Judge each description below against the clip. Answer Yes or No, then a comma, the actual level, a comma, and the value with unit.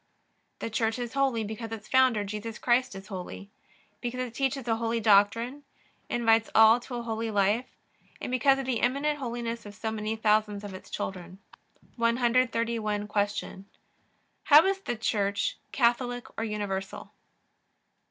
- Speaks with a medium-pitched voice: No, high, 230 Hz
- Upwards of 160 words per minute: No, average, 150 wpm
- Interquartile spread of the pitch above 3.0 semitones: No, narrow, 2.6 semitones